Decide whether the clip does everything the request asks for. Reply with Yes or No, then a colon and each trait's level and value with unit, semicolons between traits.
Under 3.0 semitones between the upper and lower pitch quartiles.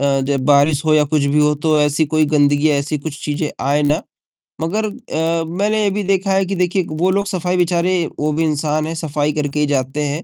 No: average, 3.4 semitones